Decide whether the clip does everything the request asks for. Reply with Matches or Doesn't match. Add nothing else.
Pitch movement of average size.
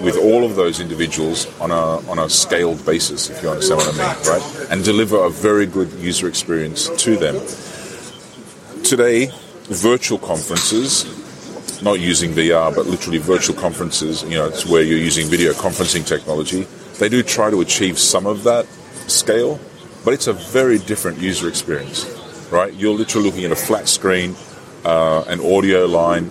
Matches